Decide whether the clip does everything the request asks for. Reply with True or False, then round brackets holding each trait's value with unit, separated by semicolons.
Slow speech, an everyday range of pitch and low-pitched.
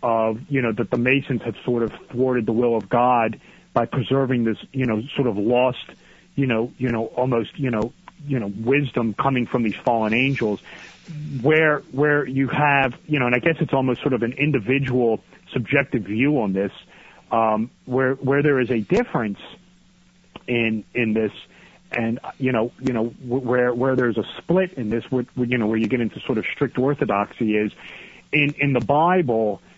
False (185 wpm; 3.2 semitones; 125 Hz)